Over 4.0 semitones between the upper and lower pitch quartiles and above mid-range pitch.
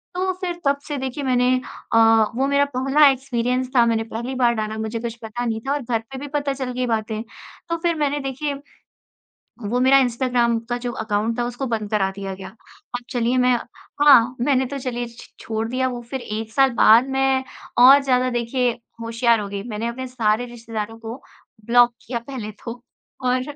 No: narrow, 2.6 semitones; high, 245 Hz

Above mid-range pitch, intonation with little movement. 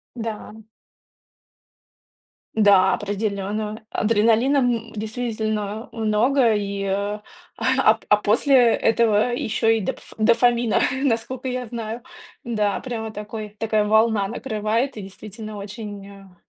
Yes: high, 220 Hz; narrow, 2.0 semitones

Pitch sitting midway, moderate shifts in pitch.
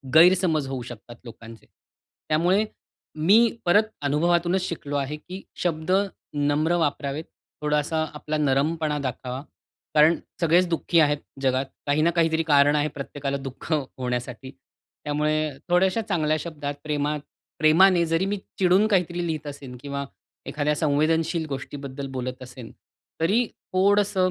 Yes: medium, 150 Hz; average, 3.4 semitones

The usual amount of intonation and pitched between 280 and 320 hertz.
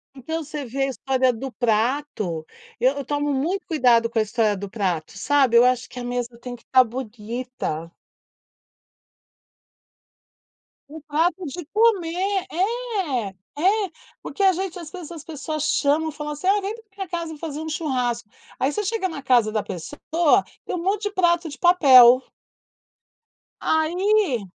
No: wide, 6.2 semitones; very high, 290 Hz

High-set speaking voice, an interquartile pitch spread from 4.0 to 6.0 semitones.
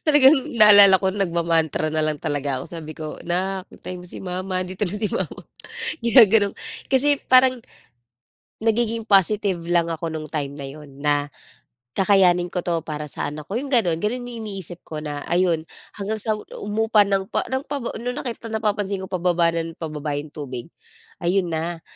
No: medium, 180 Hz; average, 5.0 semitones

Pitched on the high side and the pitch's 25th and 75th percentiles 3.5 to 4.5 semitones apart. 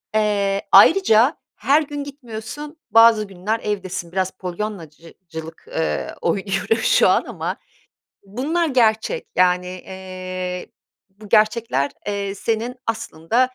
Yes: high, 210 Hz; average, 3.9 semitones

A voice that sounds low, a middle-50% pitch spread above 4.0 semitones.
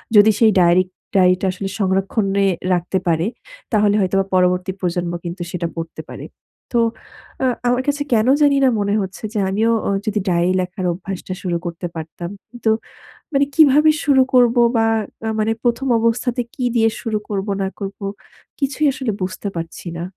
No: high, 200 Hz; average, 4.4 semitones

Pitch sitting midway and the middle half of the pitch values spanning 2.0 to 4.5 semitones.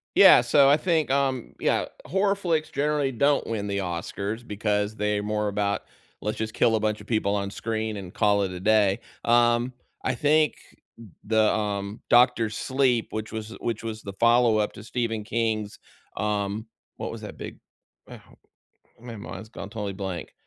No: low, 110 Hz; average, 2.8 semitones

